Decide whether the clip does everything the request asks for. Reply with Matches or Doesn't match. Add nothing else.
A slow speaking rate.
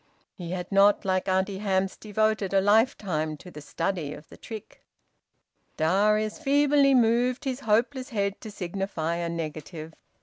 Doesn't match